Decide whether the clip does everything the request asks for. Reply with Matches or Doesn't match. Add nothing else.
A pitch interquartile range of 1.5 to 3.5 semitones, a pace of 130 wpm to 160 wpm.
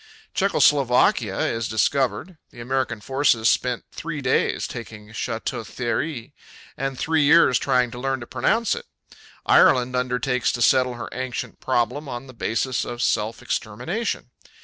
Matches